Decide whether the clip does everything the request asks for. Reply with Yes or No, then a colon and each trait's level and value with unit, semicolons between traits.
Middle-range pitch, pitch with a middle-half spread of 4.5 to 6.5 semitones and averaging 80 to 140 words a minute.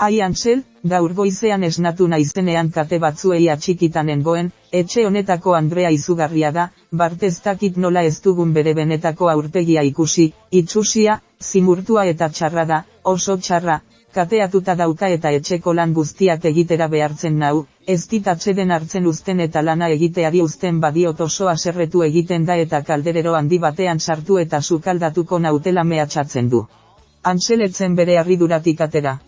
No: medium, 170 Hz; narrow, 2.6 semitones; average, 135 wpm